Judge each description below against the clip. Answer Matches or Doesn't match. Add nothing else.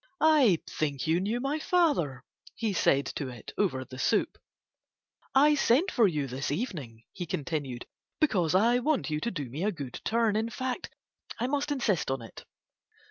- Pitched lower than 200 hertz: Matches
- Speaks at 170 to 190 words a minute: Matches